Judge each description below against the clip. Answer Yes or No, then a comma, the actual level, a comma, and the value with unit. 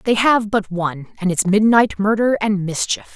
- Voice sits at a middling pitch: No, high, 205 Hz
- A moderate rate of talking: Yes, average, 190 wpm